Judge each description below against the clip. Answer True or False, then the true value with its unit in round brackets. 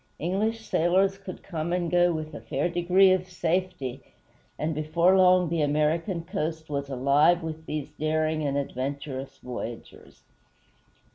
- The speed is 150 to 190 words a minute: False (140 wpm)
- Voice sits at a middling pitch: True (160 Hz)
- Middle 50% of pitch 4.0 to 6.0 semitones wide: False (3.5 semitones)